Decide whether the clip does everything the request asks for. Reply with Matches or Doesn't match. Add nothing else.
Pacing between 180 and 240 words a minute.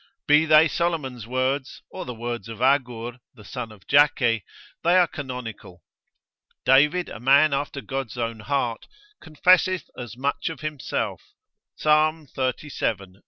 Doesn't match